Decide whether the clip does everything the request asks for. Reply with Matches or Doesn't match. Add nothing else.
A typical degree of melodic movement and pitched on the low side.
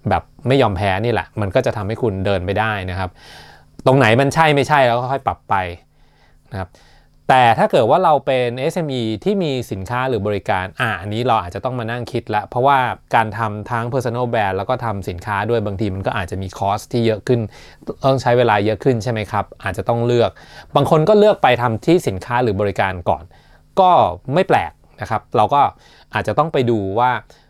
Matches